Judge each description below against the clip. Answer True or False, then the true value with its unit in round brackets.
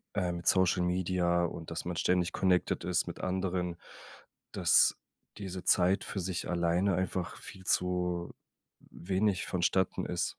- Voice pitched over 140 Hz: False (90 Hz)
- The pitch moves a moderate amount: False (1.2 semitones)